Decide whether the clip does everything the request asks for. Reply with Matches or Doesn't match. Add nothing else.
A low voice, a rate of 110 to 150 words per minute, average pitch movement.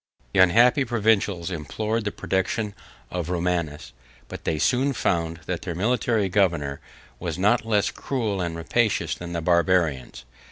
Matches